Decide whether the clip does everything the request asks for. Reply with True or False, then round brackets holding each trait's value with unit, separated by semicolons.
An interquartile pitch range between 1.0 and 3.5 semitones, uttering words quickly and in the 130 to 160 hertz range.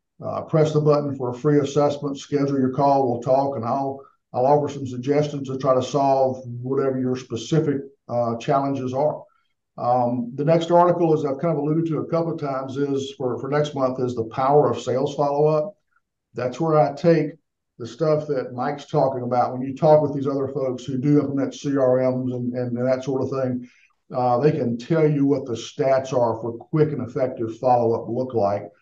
True (2.8 semitones; 210 wpm; 135 Hz)